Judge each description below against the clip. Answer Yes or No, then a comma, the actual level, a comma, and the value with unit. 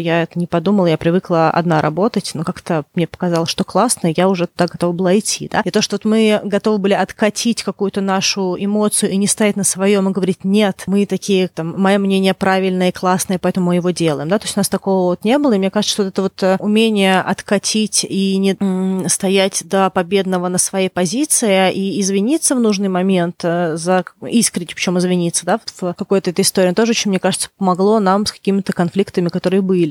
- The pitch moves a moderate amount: No, narrow, 1.9 semitones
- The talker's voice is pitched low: No, high, 190 Hz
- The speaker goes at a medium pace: No, fast, 205 wpm